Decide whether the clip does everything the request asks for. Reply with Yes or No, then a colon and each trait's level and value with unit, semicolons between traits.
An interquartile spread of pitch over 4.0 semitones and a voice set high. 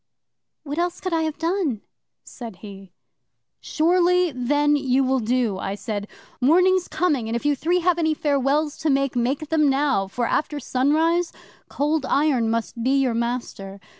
Yes: average, 4.9 semitones; very high, 280 Hz